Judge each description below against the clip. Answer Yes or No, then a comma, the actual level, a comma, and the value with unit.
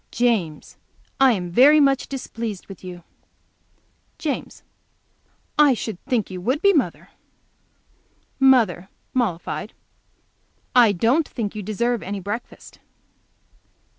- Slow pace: Yes, slow, 105 wpm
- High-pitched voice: Yes, high, 230 Hz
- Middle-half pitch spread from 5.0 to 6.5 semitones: Yes, wide, 5.5 semitones